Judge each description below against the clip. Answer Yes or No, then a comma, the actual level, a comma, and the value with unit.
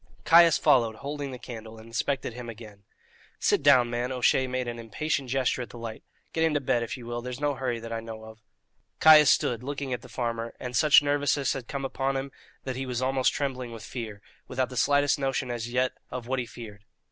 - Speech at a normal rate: No, fast, 225 wpm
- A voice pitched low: Yes, low, 125 Hz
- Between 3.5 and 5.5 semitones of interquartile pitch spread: No, average, 2.8 semitones